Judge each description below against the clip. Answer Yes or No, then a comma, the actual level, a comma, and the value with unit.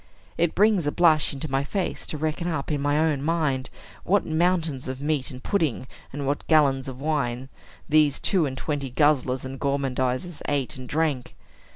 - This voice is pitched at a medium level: Yes, medium, 145 Hz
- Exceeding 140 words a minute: Yes, average, 180 wpm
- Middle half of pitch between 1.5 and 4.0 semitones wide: Yes, average, 2.9 semitones